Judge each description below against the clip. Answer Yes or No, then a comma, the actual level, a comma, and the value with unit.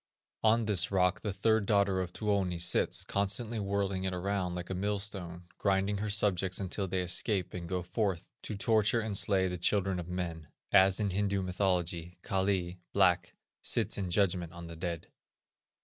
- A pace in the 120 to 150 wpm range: No, average, 170 wpm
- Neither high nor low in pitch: No, very low, 95 Hz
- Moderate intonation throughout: No, narrow, 2.1 semitones